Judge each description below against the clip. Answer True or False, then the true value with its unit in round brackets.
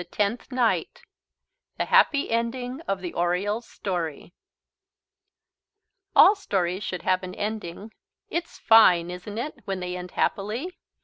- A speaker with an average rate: False (125 wpm)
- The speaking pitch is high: True (200 Hz)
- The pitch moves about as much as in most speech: True (4.5 semitones)